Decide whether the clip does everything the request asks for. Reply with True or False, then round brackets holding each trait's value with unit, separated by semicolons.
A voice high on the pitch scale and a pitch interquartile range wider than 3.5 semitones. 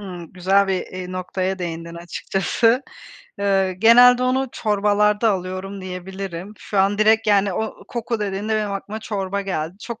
False (195 Hz; 2.5 semitones)